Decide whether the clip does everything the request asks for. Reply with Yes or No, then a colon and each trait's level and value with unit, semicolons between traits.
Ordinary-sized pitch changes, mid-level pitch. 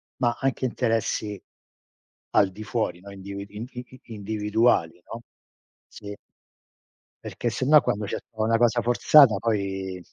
No: average, 3.1 semitones; low, 110 Hz